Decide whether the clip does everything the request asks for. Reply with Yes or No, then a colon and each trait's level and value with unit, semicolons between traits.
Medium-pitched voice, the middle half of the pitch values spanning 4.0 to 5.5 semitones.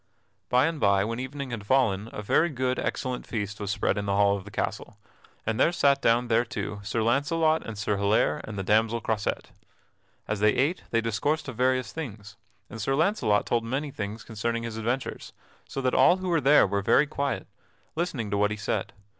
No: low, 115 Hz; average, 4.7 semitones